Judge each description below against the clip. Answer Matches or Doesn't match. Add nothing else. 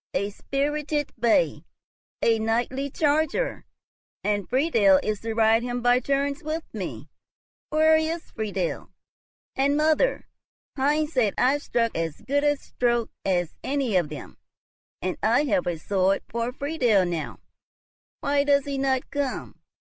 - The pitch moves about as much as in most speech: Matches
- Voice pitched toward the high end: Matches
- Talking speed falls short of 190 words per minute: Matches